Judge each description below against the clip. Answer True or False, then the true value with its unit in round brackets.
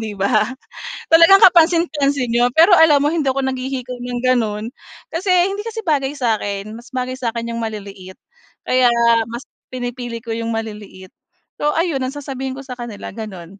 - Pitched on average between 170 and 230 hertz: False (255 Hz)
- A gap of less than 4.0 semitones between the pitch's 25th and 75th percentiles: False (4.5 semitones)